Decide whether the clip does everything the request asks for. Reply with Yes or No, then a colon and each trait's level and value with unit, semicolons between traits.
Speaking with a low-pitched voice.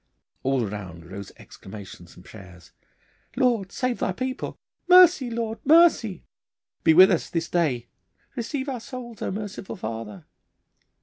No: high, 190 Hz